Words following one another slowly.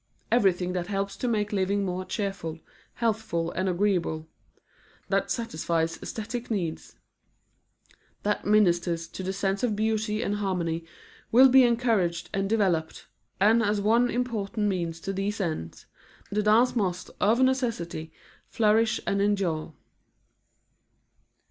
Yes: slow, 125 wpm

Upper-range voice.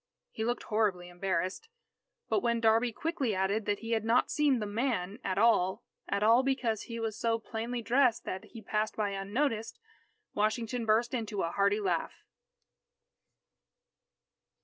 Yes: high, 220 Hz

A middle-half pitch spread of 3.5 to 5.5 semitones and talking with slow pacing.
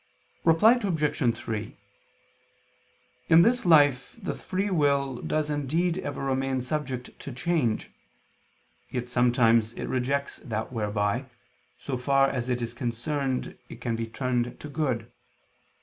Yes: average, 4.0 semitones; slow, 130 wpm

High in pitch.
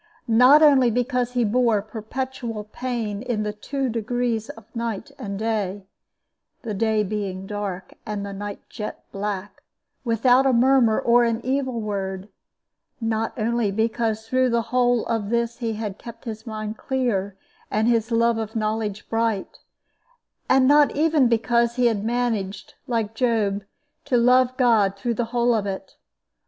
Yes: high, 225 Hz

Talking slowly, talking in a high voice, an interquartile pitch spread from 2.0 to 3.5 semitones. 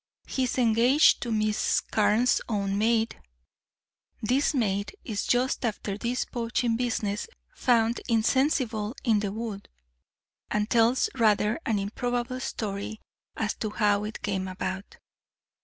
Yes: slow, 125 wpm; high, 225 Hz; average, 2.7 semitones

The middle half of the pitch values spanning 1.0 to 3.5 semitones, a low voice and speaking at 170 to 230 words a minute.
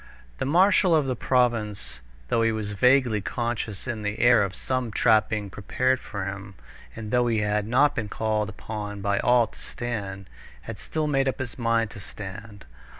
Yes: average, 3.2 semitones; low, 110 Hz; average, 185 wpm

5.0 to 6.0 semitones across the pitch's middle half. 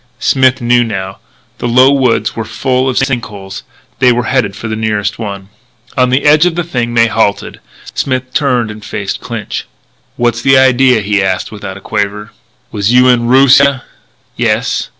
No: average, 3.7 semitones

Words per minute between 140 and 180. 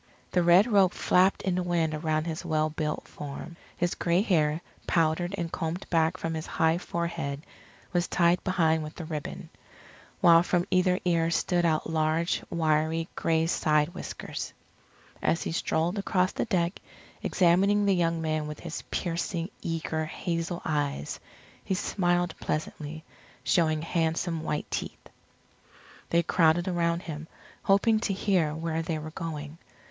Yes: average, 150 wpm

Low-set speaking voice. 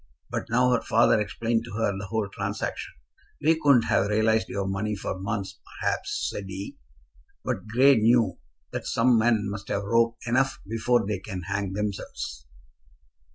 Yes: low, 110 Hz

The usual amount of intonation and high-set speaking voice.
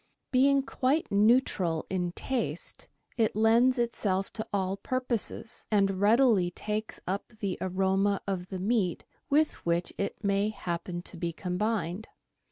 Yes: average, 3.7 semitones; high, 200 Hz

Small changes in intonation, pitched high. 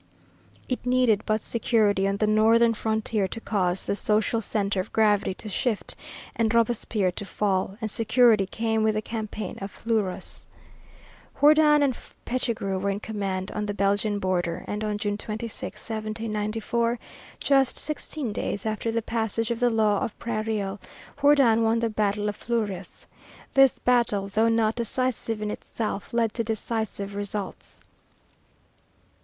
Yes: narrow, 2.1 semitones; high, 215 Hz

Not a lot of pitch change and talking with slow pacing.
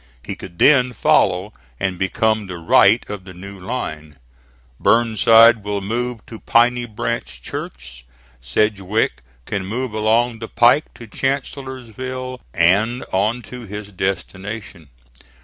No: average, 4.0 semitones; slow, 125 wpm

